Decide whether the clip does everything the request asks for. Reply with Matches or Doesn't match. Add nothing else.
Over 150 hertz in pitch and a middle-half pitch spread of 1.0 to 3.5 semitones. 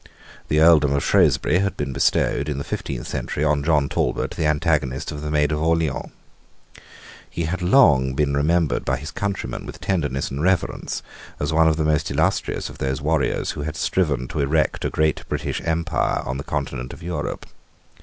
Doesn't match